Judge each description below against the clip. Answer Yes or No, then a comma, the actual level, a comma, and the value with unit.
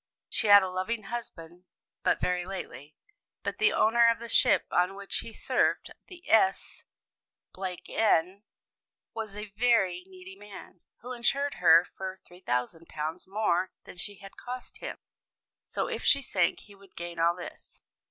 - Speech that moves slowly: No, average, 150 wpm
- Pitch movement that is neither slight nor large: Yes, average, 3.8 semitones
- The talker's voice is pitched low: No, high, 195 Hz